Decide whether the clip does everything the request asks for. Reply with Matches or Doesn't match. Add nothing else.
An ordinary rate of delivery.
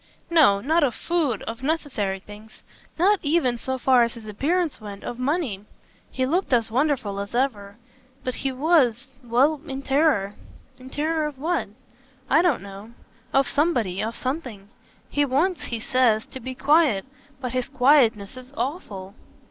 Matches